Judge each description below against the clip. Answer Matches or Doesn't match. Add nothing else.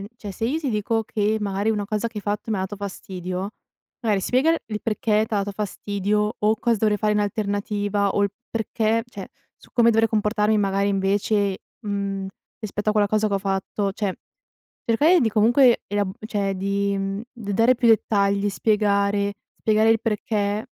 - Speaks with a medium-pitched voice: Doesn't match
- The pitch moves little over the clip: Matches